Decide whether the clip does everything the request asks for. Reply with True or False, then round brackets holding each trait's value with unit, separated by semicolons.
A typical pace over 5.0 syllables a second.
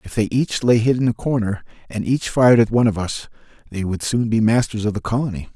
True (6.2 syllables/s)